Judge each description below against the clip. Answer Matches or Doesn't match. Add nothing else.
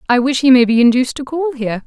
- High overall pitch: Matches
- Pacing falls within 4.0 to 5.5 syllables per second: Doesn't match